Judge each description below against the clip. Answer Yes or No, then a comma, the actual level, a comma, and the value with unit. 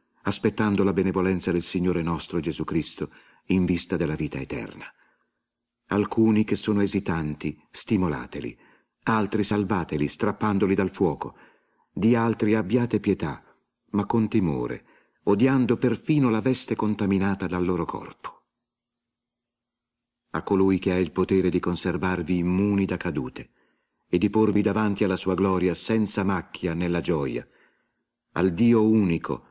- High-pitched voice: No, low, 100 Hz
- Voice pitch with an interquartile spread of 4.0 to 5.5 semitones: No, average, 3.4 semitones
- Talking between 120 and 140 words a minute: Yes, average, 130 wpm